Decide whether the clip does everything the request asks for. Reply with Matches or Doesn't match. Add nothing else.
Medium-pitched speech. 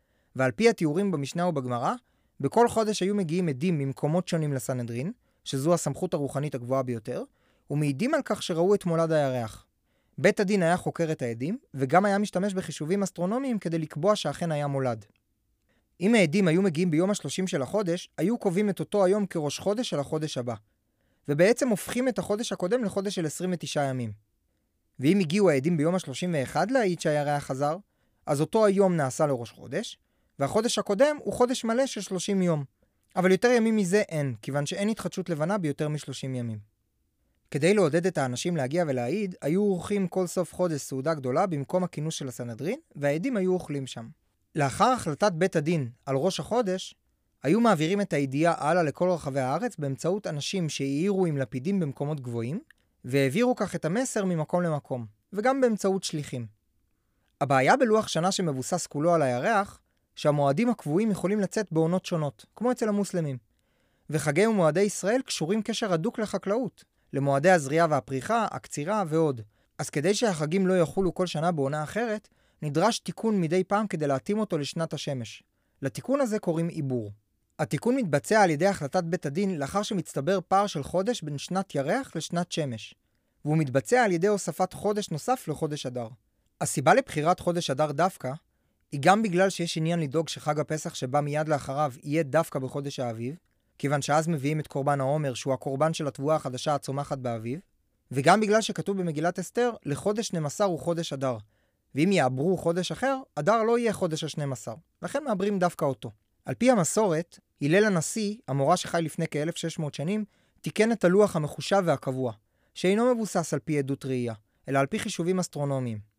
Matches